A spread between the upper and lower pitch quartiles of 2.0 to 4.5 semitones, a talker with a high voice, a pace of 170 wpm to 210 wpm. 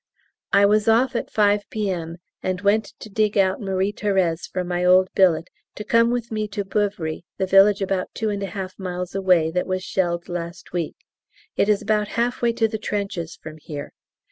Yes: average, 2.7 semitones; high, 195 Hz; average, 195 wpm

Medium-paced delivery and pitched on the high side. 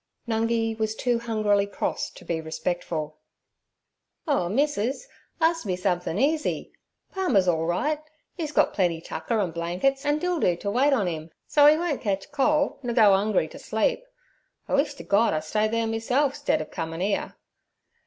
Yes: average, 170 wpm; high, 220 Hz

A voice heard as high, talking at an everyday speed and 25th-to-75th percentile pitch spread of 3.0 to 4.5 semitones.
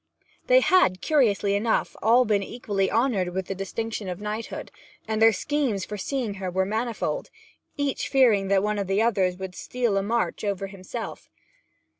Yes: high, 210 Hz; average, 170 wpm; average, 3.4 semitones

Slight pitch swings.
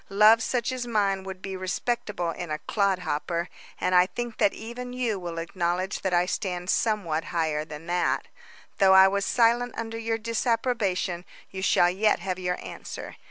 No: average, 4.1 semitones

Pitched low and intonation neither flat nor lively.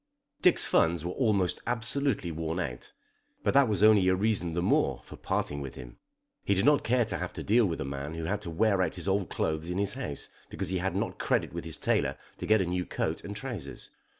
Yes: very low, 95 Hz; average, 4.7 semitones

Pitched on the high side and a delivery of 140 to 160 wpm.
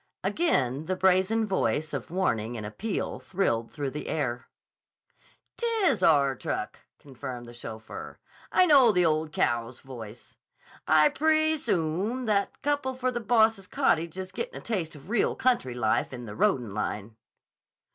No: medium, 160 Hz; average, 155 wpm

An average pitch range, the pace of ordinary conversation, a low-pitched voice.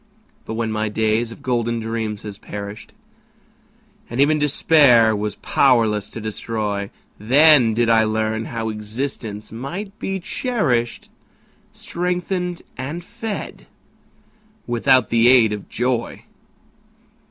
No: average, 4.5 semitones; slow, 115 wpm; low, 115 Hz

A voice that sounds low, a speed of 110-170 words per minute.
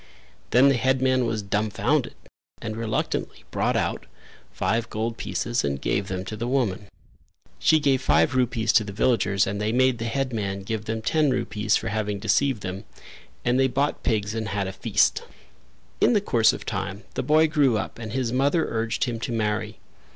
No: low, 115 Hz; average, 185 wpm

